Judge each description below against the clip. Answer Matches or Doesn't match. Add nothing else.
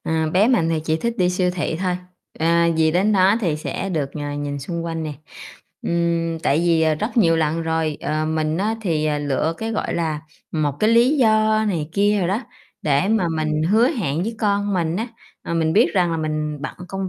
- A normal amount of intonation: Matches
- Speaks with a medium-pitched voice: Matches